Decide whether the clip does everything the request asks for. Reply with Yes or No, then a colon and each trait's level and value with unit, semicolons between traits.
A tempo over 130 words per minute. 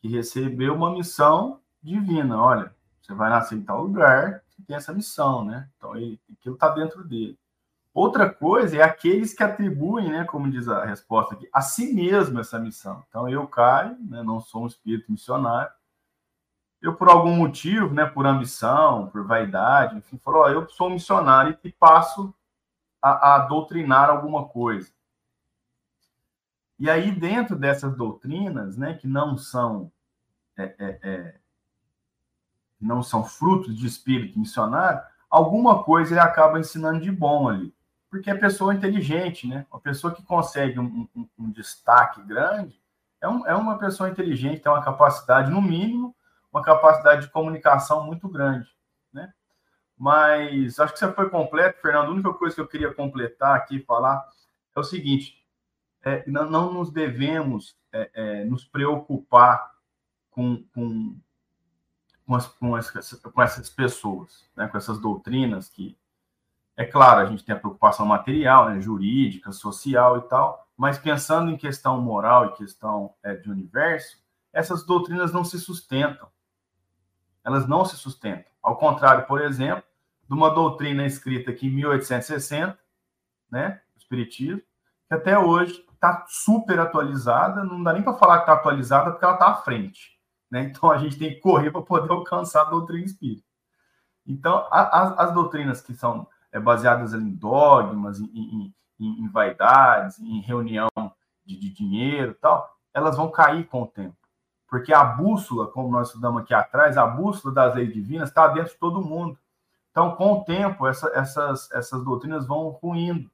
Yes: average, 160 wpm